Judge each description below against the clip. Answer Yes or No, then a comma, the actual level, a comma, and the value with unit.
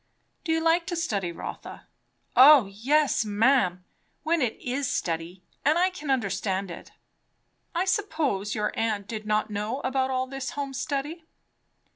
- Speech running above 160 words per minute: No, average, 150 wpm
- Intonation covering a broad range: Yes, wide, 6.7 semitones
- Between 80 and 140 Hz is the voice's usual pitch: No, very high, 260 Hz